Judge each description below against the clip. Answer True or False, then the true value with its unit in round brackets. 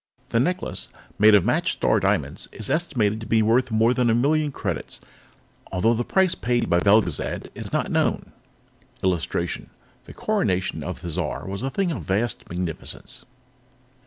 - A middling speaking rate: True (160 wpm)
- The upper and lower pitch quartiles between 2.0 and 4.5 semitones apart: False (5.1 semitones)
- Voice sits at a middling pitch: False (115 Hz)